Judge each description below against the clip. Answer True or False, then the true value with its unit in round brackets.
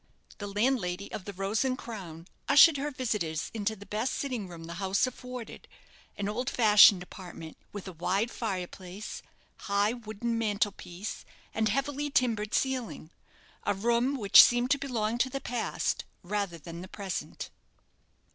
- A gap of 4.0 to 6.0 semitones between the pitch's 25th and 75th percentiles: True (4.3 semitones)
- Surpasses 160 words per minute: False (155 wpm)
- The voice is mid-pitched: False (210 Hz)